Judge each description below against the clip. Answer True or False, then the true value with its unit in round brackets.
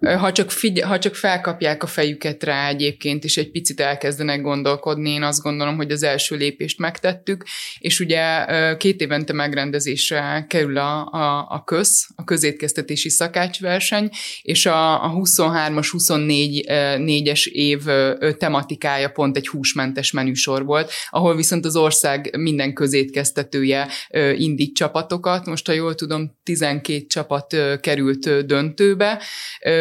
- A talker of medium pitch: True (150 Hz)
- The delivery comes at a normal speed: True (130 wpm)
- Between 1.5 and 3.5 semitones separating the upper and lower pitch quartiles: True (2.5 semitones)